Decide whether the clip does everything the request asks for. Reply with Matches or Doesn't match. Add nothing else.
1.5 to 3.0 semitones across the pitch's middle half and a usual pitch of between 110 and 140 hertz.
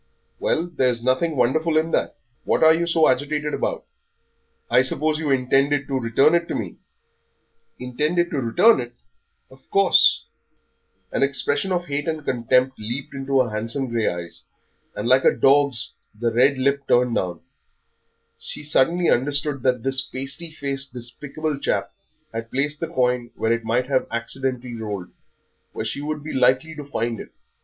Doesn't match